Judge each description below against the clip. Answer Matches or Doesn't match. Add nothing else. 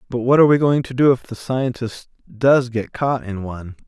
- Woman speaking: Doesn't match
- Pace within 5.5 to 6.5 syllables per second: Doesn't match